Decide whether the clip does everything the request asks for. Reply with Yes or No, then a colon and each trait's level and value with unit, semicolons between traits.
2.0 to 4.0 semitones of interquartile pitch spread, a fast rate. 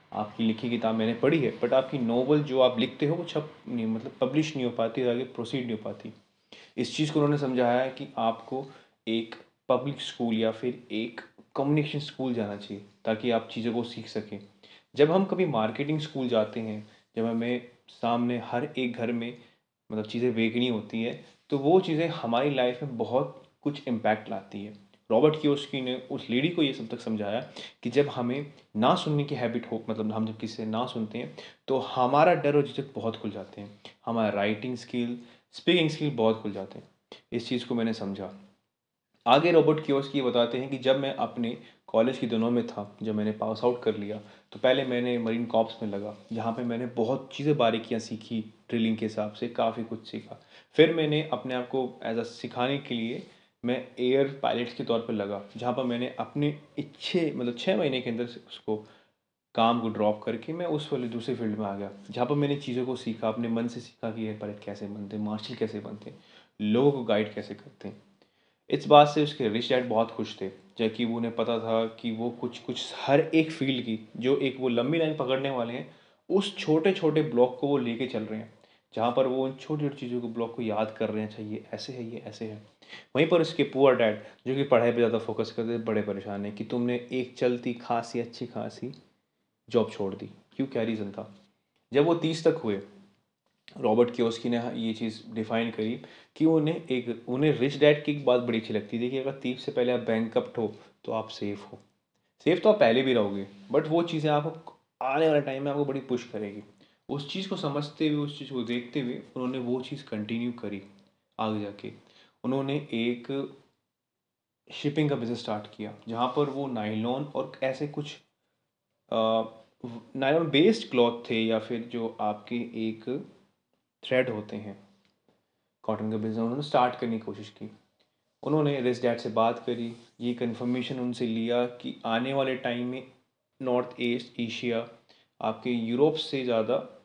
Yes: average, 3.3 semitones; fast, 200 wpm